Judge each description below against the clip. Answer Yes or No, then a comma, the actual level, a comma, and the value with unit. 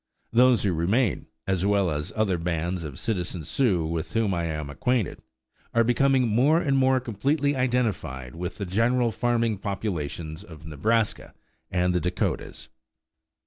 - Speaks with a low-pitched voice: Yes, low, 100 Hz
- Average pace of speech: Yes, average, 145 wpm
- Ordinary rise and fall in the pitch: No, wide, 6.2 semitones